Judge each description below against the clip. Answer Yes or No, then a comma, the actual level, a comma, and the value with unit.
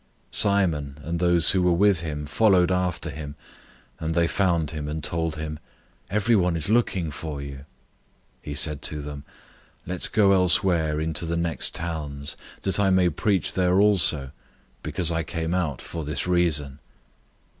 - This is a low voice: Yes, very low, 85 Hz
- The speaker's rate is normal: Yes, average, 165 wpm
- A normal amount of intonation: Yes, average, 3.3 semitones